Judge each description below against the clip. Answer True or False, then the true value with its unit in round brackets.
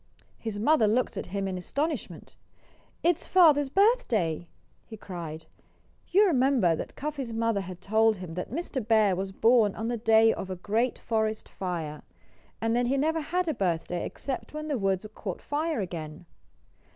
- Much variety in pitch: True (6.9 semitones)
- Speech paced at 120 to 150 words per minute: False (165 wpm)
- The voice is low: False (225 Hz)